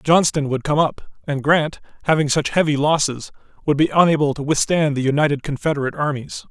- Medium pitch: Yes, medium, 145 Hz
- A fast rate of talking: No, average, 175 wpm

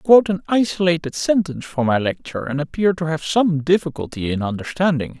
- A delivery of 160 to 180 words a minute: No, average, 195 wpm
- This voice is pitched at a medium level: Yes, medium, 160 Hz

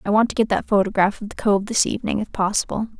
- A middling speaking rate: No, fast, 260 wpm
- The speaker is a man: No, female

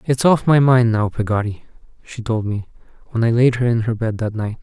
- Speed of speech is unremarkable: No, fast, 235 wpm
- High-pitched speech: No, low, 115 Hz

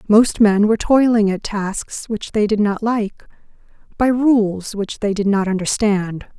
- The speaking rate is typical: Yes, average, 170 wpm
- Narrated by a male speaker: No, female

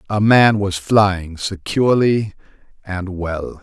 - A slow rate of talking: Yes, slow, 115 wpm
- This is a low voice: Yes, low, 100 Hz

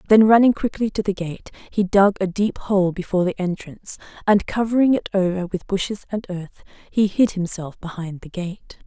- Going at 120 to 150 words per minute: No, average, 190 wpm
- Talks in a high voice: Yes, high, 195 Hz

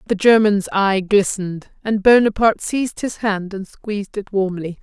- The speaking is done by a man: No, female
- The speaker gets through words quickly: No, average, 160 wpm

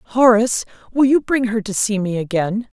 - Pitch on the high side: Yes, high, 220 Hz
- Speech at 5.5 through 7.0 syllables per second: No, 5.0 syllables/s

